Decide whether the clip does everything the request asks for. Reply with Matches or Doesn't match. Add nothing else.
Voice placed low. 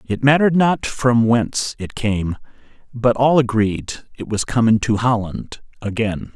Matches